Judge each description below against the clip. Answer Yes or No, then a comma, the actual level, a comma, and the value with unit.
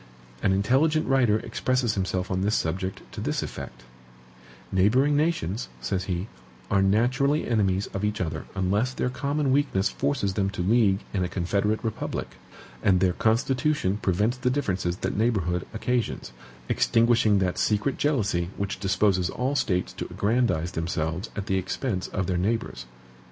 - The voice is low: Yes, low, 100 Hz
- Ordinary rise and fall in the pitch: Yes, average, 4.9 semitones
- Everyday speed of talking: Yes, average, 150 wpm